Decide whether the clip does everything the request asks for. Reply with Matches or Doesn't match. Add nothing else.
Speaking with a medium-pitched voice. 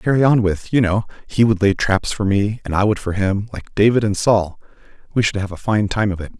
Doesn't match